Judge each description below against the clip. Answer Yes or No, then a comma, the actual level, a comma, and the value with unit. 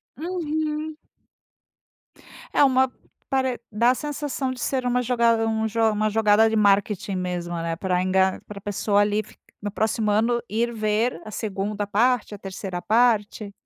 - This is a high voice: Yes, high, 220 Hz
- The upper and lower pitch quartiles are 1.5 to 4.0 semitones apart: Yes, average, 3.5 semitones